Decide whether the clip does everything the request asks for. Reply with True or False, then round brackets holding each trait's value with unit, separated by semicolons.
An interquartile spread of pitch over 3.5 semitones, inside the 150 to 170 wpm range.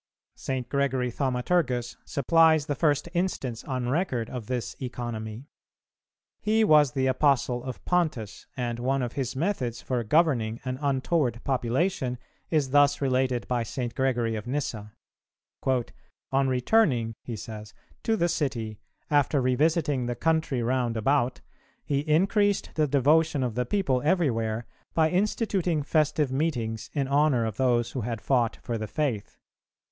False (4.1 semitones; 140 wpm)